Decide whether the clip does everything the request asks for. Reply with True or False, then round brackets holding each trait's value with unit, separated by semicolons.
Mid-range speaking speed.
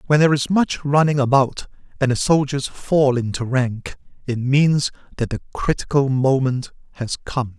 True (160 wpm)